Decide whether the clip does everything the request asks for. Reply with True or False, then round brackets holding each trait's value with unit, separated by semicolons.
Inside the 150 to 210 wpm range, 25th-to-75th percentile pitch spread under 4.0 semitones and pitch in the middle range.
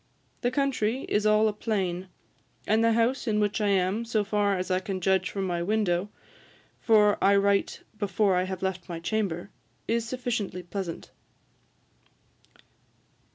False (155 wpm; 2.8 semitones; 205 Hz)